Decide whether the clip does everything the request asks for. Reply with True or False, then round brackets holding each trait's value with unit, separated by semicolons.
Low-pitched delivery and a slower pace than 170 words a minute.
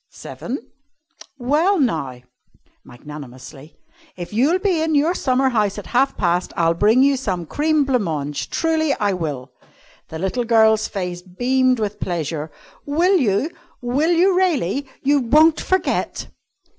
False (240 Hz; 140 wpm)